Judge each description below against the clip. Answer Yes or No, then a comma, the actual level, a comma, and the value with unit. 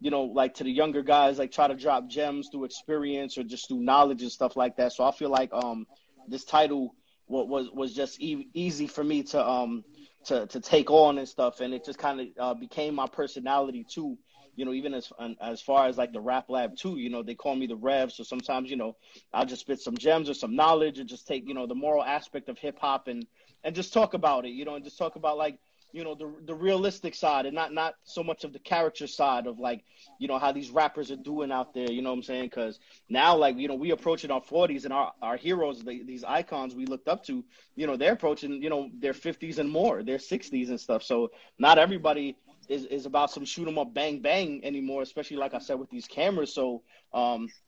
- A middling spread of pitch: Yes, average, 3.1 semitones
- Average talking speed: No, fast, 250 wpm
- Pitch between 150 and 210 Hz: No, medium, 140 Hz